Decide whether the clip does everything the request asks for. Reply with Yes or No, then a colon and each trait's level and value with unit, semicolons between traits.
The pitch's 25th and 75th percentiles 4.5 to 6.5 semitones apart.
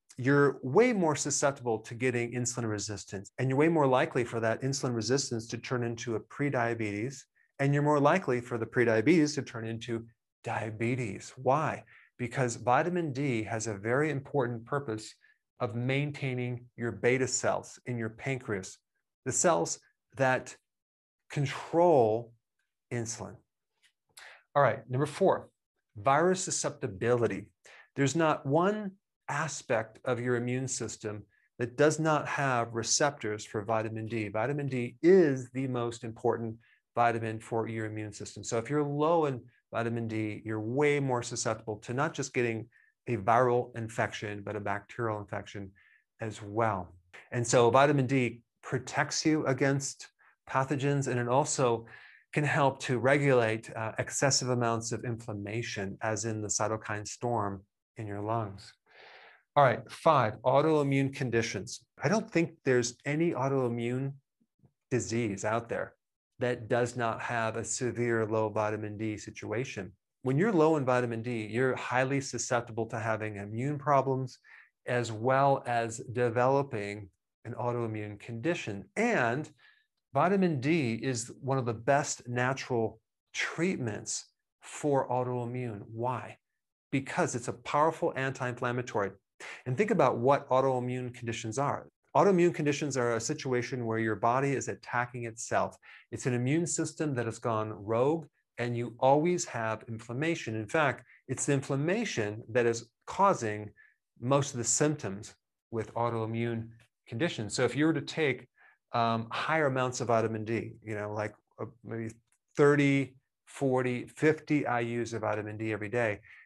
No: average, 3.5 semitones